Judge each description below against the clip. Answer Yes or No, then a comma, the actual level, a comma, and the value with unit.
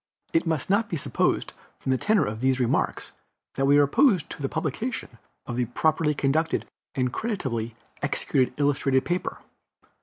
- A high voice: No, medium, 145 Hz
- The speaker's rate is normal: Yes, average, 160 wpm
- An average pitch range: Yes, average, 4.1 semitones